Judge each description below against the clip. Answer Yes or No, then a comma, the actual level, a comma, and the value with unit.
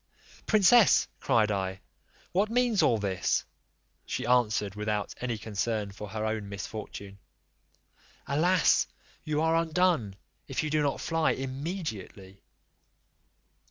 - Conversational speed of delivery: No, slow, 115 wpm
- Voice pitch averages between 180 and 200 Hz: No, low, 120 Hz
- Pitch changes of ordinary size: No, wide, 7.9 semitones